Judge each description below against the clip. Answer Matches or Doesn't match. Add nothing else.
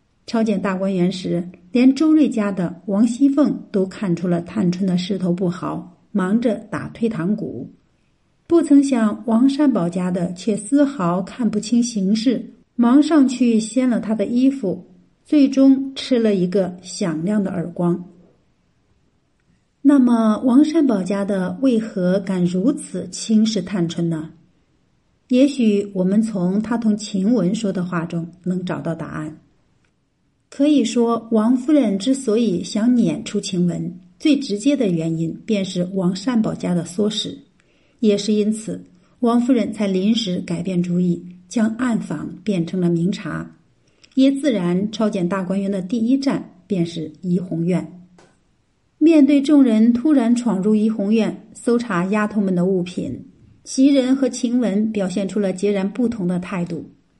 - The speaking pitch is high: Matches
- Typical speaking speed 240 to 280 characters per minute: Doesn't match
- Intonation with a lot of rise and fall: Doesn't match